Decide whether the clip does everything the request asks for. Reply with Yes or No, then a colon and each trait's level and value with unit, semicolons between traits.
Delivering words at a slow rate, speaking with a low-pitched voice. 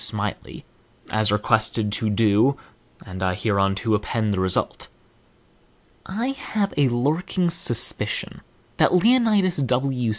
Yes: slow, 110 wpm; low, 120 Hz